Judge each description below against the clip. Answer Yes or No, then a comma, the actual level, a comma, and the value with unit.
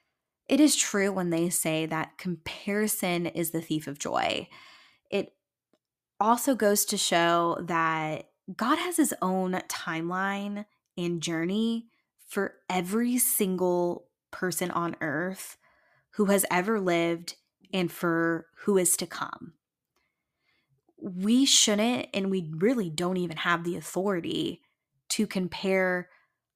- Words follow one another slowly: Yes, slow, 120 wpm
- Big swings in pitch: No, average, 3.4 semitones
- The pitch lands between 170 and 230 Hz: Yes, medium, 185 Hz